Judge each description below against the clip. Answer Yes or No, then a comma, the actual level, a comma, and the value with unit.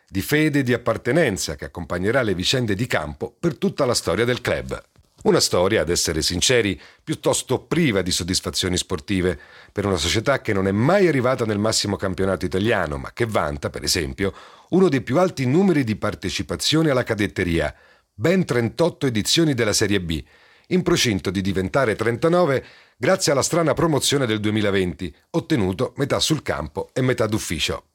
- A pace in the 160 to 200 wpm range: Yes, average, 165 wpm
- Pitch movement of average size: No, wide, 7.2 semitones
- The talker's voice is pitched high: No, low, 110 Hz